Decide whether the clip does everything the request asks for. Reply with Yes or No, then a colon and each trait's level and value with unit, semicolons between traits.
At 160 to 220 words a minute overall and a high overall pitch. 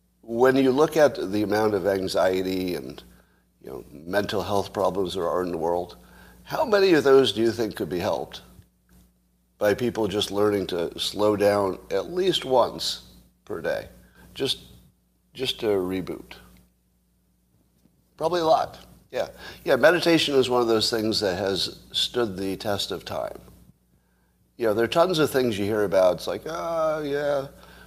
No: average, 165 wpm; low, 100 Hz